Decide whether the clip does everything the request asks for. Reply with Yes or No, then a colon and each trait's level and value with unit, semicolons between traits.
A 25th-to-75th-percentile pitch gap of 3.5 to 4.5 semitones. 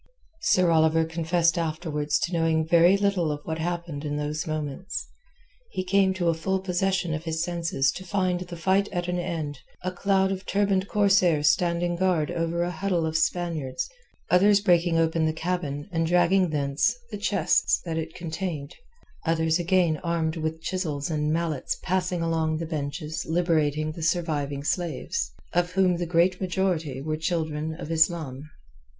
No: narrow, 2.4 semitones